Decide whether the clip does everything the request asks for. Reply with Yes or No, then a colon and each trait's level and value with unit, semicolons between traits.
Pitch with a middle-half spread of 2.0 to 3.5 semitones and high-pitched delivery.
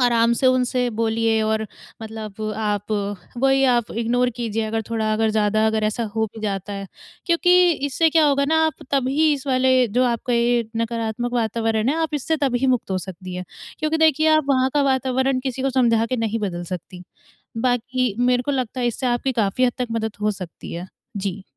Yes: average, 3.1 semitones; high, 240 Hz